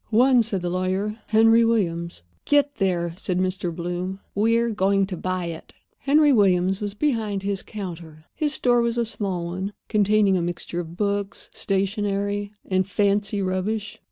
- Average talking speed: Yes, average, 155 wpm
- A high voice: Yes, high, 200 Hz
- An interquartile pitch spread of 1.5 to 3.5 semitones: Yes, average, 2.8 semitones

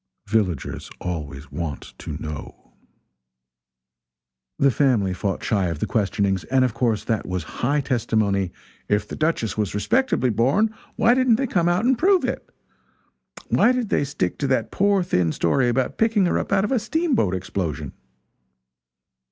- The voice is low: Yes, low, 120 Hz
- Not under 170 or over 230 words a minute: No, average, 160 wpm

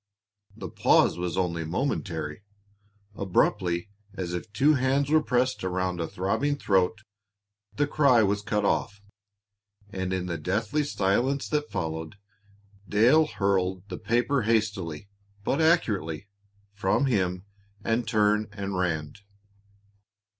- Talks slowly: Yes, slow, 120 wpm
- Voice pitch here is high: No, low, 100 Hz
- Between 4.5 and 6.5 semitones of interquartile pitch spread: Yes, average, 5.1 semitones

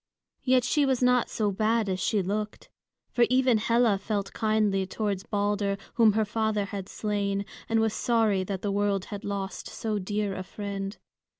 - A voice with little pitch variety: Yes, narrow, 2.0 semitones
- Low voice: No, high, 210 Hz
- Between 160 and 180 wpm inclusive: Yes, average, 175 wpm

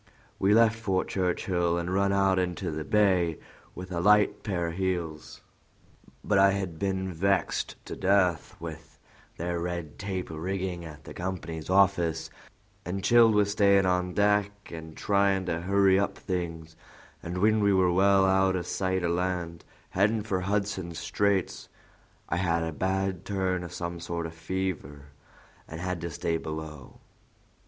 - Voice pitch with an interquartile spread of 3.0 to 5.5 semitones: No, narrow, 2.6 semitones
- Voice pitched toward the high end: No, very low, 90 Hz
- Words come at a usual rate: Yes, average, 160 wpm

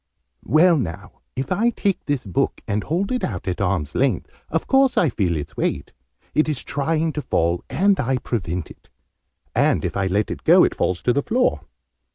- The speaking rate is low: No, average, 195 wpm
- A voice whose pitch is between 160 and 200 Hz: No, low, 130 Hz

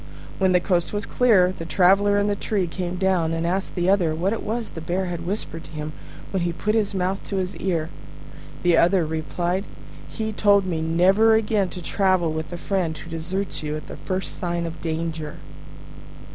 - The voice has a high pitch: No, medium, 180 Hz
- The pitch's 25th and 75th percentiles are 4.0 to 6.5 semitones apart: No, average, 3.0 semitones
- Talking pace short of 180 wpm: No, average, 200 wpm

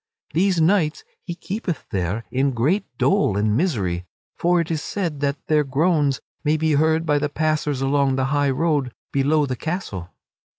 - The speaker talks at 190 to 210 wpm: No, average, 170 wpm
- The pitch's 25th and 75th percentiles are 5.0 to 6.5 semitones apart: No, average, 3.5 semitones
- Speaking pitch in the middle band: Yes, medium, 150 Hz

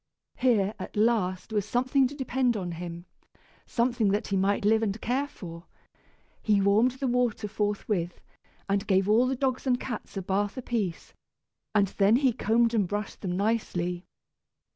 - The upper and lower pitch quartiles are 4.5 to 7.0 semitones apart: No, average, 3.8 semitones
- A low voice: No, high, 210 Hz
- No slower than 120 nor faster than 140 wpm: No, average, 165 wpm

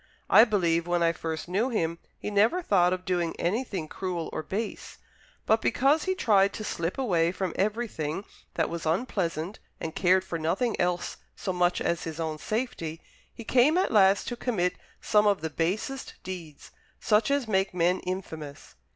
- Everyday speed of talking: Yes, average, 175 wpm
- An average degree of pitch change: Yes, average, 4.3 semitones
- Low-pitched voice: No, medium, 185 Hz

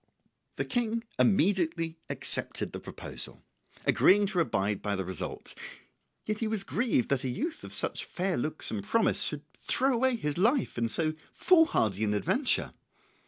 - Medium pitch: Yes, medium, 180 Hz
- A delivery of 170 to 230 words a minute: No, average, 160 wpm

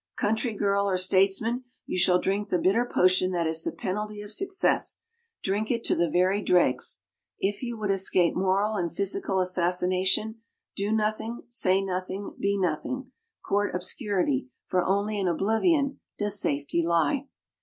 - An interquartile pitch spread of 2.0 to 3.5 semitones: Yes, average, 2.8 semitones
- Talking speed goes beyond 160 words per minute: No, average, 155 wpm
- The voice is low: No, high, 195 Hz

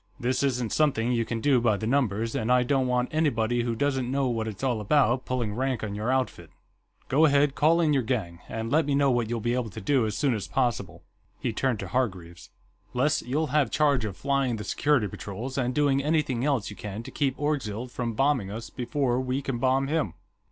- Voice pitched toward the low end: Yes, low, 125 Hz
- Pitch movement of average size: Yes, average, 3.7 semitones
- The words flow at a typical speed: No, fast, 220 wpm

